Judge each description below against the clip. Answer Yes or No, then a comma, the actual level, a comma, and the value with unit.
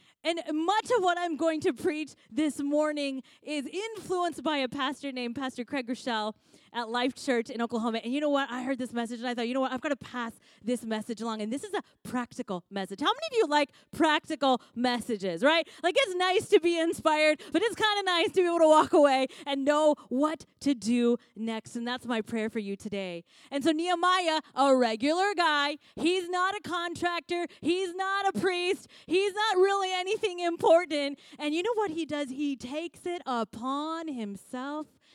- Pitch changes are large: Yes, wide, 5.9 semitones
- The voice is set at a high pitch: Yes, very high, 295 Hz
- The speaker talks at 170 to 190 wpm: No, fast, 205 wpm